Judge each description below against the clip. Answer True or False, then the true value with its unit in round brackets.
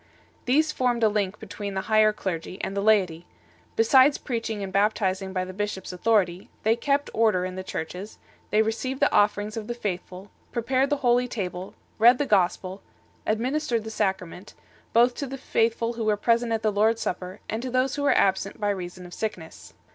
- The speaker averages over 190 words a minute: True (200 wpm)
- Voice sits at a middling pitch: False (215 Hz)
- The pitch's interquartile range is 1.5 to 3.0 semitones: False (3.8 semitones)